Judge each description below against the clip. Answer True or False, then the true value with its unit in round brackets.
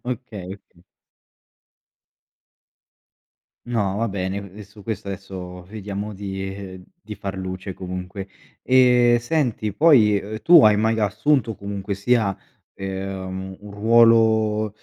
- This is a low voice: True (100 Hz)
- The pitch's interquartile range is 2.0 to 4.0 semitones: True (2.7 semitones)